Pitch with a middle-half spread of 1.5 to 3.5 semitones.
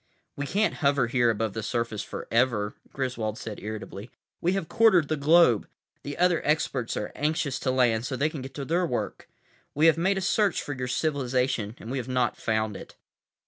No: average, 5.2 semitones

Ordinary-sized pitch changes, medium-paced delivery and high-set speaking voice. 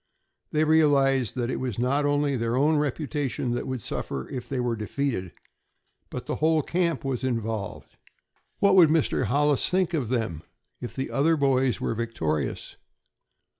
No: average, 3.9 semitones; average, 160 wpm; low, 135 Hz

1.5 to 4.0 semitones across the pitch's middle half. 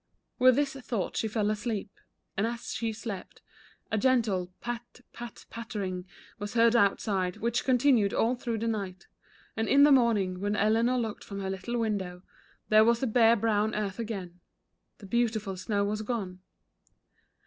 Yes: average, 2.9 semitones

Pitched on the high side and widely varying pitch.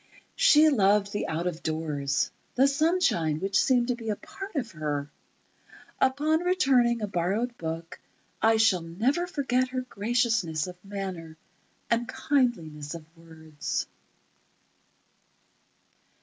Yes: high, 205 Hz; wide, 7.6 semitones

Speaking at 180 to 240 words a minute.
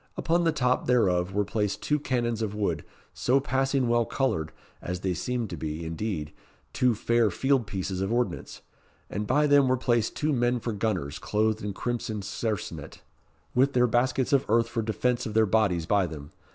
Yes: average, 185 wpm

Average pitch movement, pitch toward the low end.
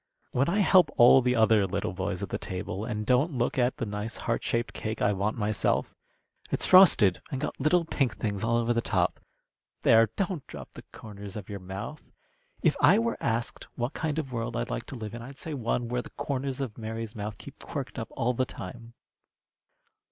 Yes: average, 4.0 semitones; low, 115 Hz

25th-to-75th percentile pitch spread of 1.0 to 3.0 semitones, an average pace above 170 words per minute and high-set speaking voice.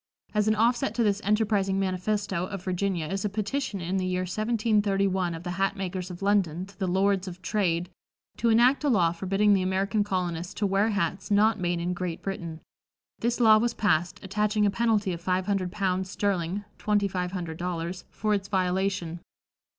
Yes: narrow, 2.5 semitones; average, 190 wpm; high, 195 Hz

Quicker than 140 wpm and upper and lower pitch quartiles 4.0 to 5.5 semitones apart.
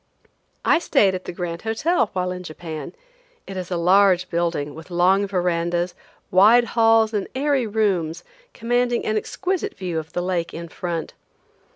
Yes: average, 160 wpm; average, 4.3 semitones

